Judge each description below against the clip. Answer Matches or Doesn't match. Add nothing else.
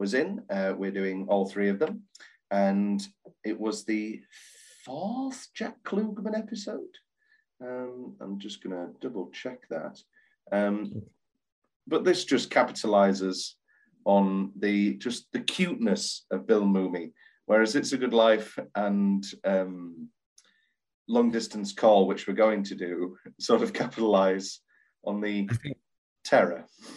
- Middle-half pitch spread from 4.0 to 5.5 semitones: Matches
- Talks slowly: Matches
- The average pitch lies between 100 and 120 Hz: Matches